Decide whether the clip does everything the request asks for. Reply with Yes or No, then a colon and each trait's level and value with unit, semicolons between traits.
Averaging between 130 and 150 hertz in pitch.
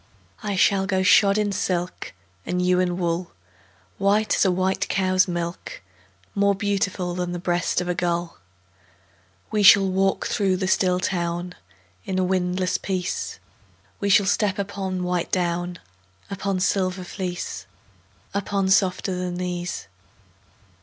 No: medium, 185 Hz